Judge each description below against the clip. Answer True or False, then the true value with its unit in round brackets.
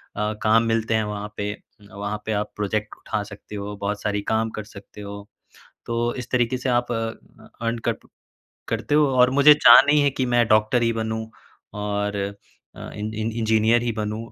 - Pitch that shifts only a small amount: True (2.2 semitones)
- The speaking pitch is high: False (110 Hz)